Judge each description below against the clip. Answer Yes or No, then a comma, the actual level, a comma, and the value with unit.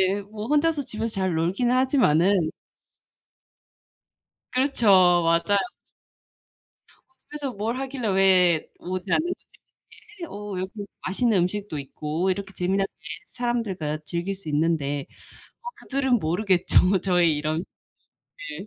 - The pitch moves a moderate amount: No, wide, 5.7 semitones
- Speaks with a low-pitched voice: No, high, 195 Hz